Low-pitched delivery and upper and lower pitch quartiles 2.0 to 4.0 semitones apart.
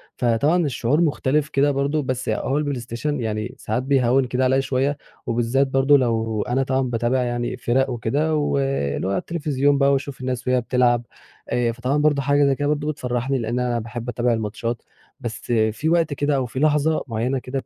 Yes: low, 130 Hz; average, 3.0 semitones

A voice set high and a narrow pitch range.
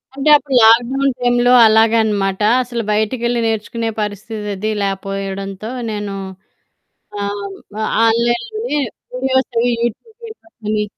No: high, 225 Hz; average, 3.1 semitones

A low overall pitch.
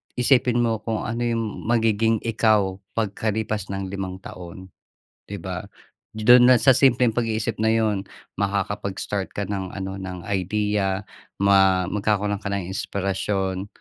Yes: low, 100 Hz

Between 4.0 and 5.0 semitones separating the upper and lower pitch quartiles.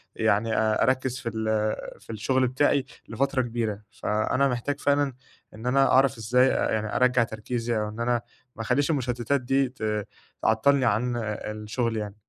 No: average, 3.1 semitones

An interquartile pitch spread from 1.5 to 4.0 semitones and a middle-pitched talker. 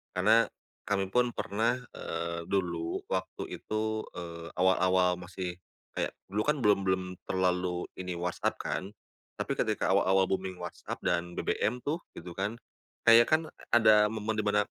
No: average, 3.3 semitones; very low, 95 Hz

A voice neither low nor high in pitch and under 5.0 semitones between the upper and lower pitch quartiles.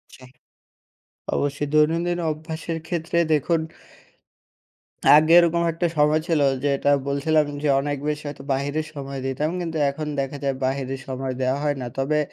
Yes: medium, 150 Hz; narrow, 2.5 semitones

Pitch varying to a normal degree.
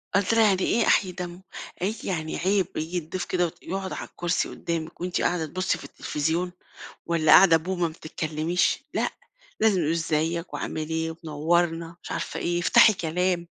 No: narrow, 2.1 semitones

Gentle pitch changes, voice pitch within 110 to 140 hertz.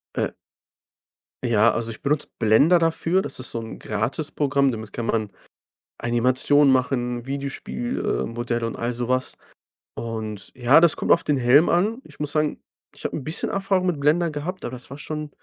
No: average, 4.7 semitones; low, 135 Hz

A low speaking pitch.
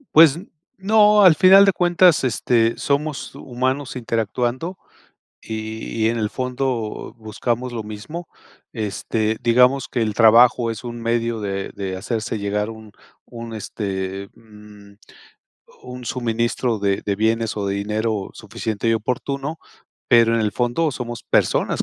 Yes: low, 115 Hz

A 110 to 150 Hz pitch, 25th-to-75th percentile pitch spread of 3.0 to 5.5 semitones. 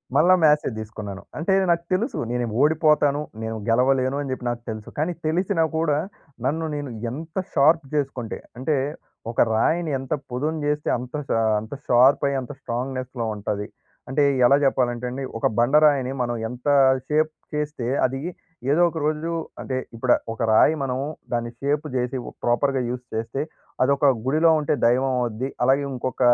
Yes: low, 135 Hz; average, 3.7 semitones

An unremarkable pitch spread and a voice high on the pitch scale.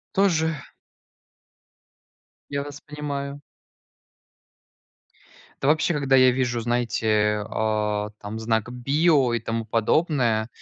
No: average, 4.6 semitones; low, 125 Hz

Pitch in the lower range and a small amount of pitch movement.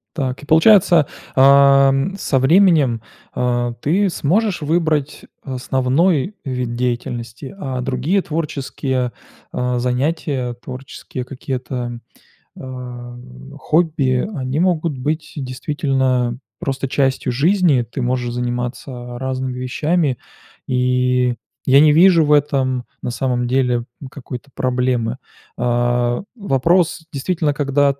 No: low, 130 Hz; average, 3.3 semitones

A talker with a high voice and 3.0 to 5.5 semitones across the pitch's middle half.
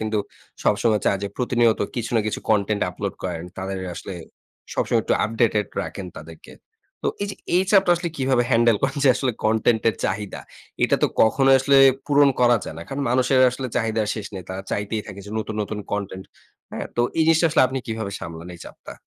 No: low, 110 Hz; average, 4.3 semitones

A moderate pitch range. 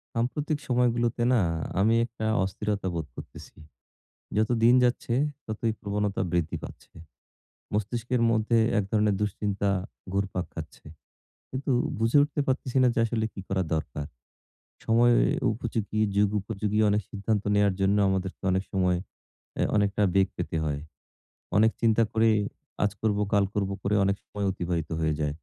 Yes: average, 3.0 semitones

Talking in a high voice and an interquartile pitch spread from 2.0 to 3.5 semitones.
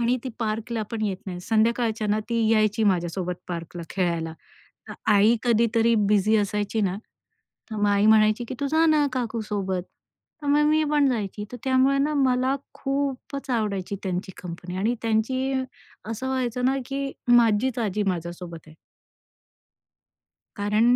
No: high, 220 Hz; average, 4.1 semitones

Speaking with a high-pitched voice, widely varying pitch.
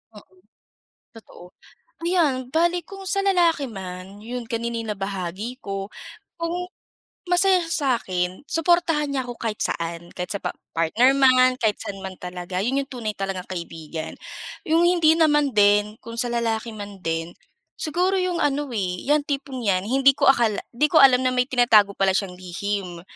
Yes: high, 235 Hz; wide, 7.1 semitones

